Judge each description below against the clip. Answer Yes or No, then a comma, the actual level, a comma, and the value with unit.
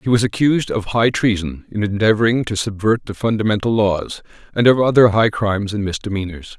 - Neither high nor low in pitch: No, low, 105 Hz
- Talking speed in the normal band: Yes, average, 180 wpm